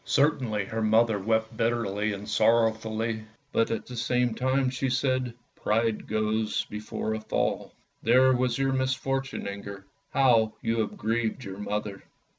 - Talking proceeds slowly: No, average, 150 wpm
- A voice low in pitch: Yes, low, 115 Hz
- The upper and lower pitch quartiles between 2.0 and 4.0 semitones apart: Yes, average, 2.7 semitones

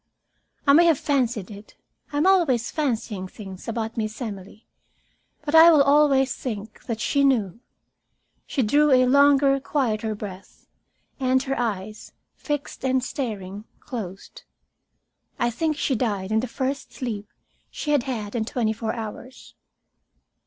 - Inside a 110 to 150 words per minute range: Yes, average, 145 wpm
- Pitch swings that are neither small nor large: Yes, average, 4.6 semitones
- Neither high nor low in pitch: No, high, 245 Hz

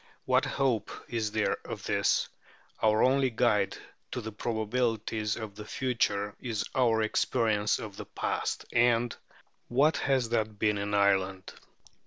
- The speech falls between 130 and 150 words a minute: Yes, average, 140 wpm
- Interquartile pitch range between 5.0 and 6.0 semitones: No, average, 2.7 semitones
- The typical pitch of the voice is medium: No, low, 110 Hz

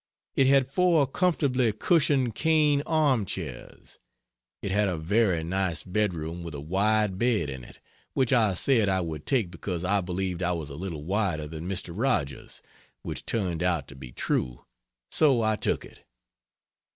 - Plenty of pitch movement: Yes, wide, 6.9 semitones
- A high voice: No, very low, 95 Hz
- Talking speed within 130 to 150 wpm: No, average, 165 wpm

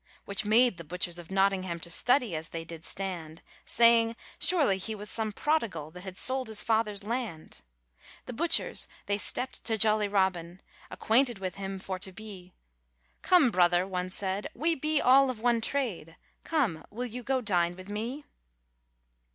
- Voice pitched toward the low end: No, high, 205 Hz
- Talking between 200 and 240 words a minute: No, average, 165 wpm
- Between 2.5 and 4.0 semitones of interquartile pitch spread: No, average, 4.9 semitones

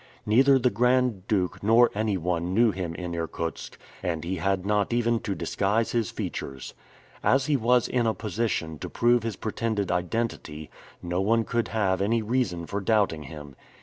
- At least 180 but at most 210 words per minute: No, average, 170 wpm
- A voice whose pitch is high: No, low, 105 Hz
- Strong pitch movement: No, average, 4.7 semitones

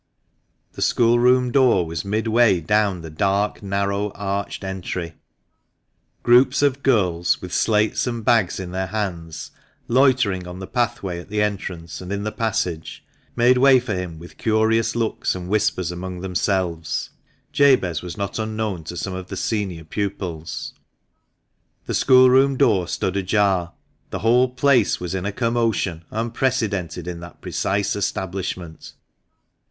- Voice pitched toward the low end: Yes, low, 100 Hz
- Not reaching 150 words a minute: Yes, average, 140 wpm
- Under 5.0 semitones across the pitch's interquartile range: Yes, average, 4.2 semitones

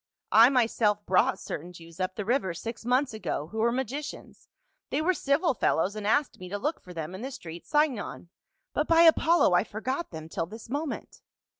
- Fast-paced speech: Yes, fast, 210 wpm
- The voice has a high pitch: Yes, high, 225 Hz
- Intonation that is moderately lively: No, wide, 7.2 semitones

